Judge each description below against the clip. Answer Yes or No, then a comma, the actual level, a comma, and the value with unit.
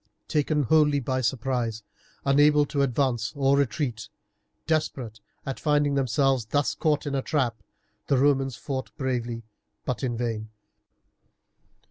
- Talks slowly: Yes, slow, 125 wpm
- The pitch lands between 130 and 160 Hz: Yes, low, 135 Hz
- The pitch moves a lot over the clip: No, average, 3.3 semitones